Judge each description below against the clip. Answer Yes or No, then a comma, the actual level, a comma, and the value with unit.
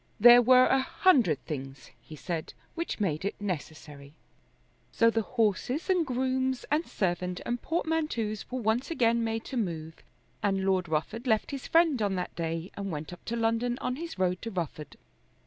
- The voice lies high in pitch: Yes, high, 220 Hz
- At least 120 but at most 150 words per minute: No, average, 170 wpm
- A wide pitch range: Yes, wide, 6.5 semitones